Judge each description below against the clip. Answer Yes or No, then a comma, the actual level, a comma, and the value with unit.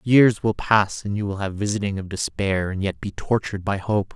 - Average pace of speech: No, fast, 230 wpm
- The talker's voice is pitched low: Yes, low, 100 Hz